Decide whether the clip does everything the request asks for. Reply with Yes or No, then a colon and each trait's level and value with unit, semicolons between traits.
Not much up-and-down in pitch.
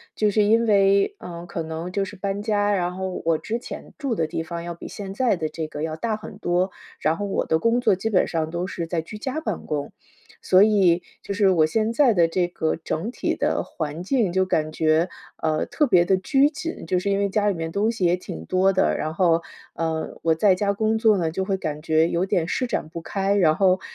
No: average, 4.0 semitones